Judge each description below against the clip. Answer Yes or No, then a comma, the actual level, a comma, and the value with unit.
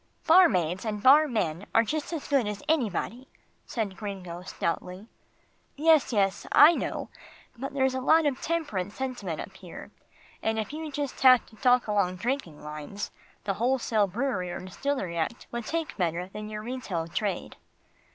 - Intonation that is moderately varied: No, wide, 6.3 semitones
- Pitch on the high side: Yes, high, 220 Hz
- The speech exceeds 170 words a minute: No, average, 160 wpm